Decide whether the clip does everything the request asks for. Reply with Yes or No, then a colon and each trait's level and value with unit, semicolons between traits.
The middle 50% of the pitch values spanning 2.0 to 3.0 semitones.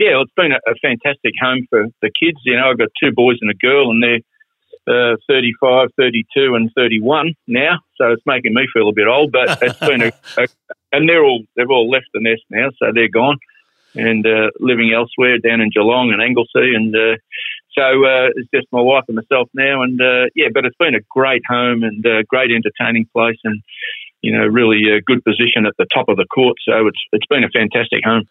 Yes: average, 2.7 semitones